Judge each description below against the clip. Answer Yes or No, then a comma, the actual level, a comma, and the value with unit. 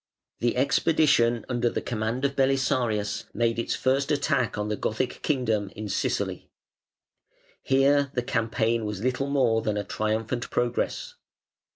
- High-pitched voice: No, low, 120 Hz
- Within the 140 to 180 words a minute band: Yes, average, 145 wpm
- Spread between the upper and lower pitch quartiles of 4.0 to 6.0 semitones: No, average, 3.5 semitones